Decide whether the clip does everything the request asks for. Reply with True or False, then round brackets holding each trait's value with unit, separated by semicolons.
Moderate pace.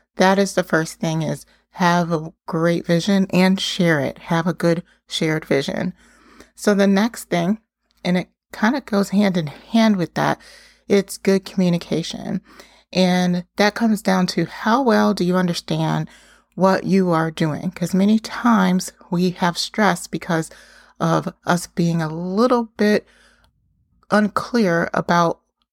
True (150 wpm)